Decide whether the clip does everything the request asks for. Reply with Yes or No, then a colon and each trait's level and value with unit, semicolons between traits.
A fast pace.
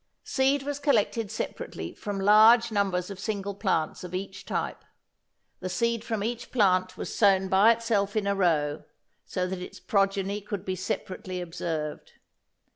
No: average, 155 wpm